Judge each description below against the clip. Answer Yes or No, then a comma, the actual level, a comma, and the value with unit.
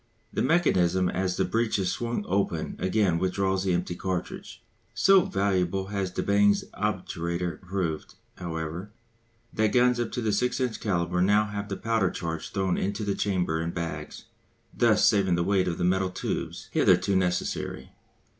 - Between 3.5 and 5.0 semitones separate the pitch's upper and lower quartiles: No, narrow, 2.6 semitones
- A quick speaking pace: No, average, 165 wpm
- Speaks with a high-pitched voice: No, very low, 95 Hz